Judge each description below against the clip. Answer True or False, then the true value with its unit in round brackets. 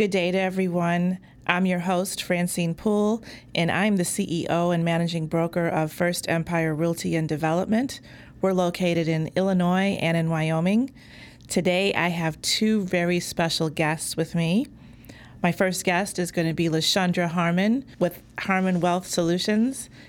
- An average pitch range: False (2.1 semitones)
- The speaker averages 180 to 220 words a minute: False (150 wpm)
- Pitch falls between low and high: True (175 Hz)